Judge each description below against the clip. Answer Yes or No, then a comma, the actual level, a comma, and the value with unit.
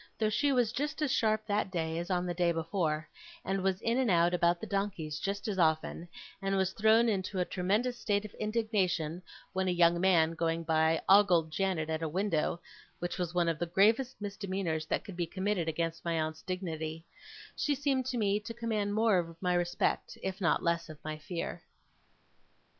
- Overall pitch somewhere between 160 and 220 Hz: Yes, medium, 185 Hz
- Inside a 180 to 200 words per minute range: Yes, average, 195 wpm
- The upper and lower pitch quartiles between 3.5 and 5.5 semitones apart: Yes, average, 3.8 semitones